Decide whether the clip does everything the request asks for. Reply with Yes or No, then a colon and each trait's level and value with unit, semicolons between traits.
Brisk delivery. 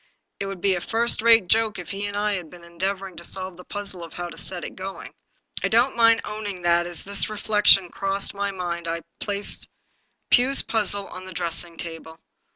Yes: fast, 210 wpm